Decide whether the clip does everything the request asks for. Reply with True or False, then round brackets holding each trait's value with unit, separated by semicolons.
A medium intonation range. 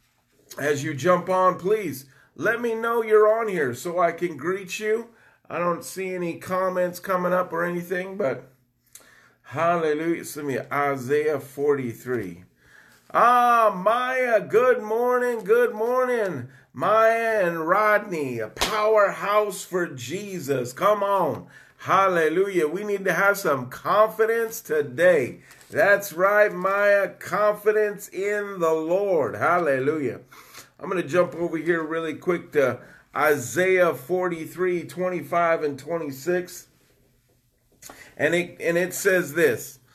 True (4.8 semitones)